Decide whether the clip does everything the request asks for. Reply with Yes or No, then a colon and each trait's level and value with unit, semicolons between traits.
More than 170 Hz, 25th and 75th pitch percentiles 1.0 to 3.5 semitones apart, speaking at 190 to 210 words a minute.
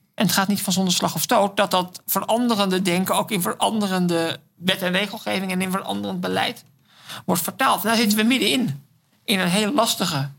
Yes: high, 190 Hz; average, 3.2 semitones; fast, 200 wpm